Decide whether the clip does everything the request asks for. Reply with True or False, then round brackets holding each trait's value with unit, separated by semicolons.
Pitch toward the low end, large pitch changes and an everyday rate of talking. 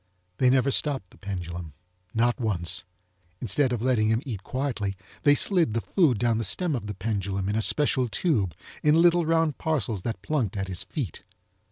True (115 Hz; 6.3 semitones; 185 wpm)